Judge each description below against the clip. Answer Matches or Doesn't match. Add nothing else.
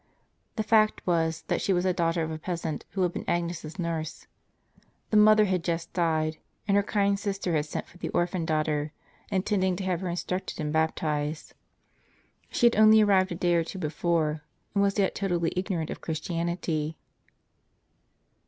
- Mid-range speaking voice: Matches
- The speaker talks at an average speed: Matches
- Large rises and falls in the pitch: Doesn't match